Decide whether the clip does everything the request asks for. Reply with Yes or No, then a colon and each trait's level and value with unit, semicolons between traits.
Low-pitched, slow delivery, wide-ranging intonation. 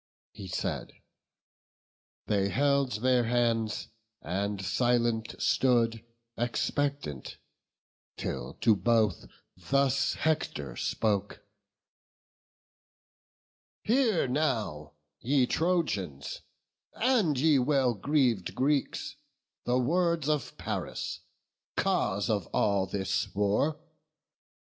Yes: low, 120 Hz; slow, 85 wpm; wide, 5.8 semitones